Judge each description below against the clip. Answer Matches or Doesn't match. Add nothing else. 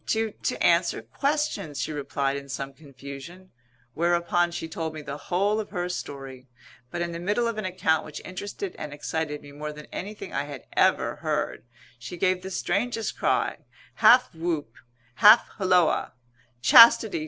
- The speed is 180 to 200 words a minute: Doesn't match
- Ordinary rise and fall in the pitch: Matches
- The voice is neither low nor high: Matches